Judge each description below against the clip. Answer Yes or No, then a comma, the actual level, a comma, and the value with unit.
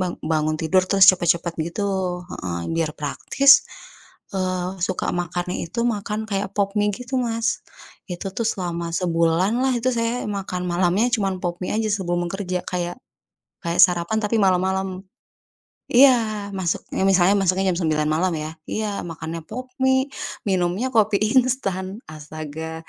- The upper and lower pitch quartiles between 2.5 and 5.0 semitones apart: Yes, average, 3.4 semitones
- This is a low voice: No, medium, 185 Hz